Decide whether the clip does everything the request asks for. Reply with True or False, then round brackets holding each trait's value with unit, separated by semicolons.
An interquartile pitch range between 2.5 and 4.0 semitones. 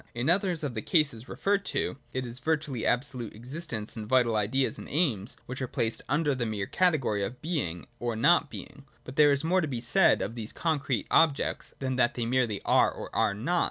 False (4.8 semitones)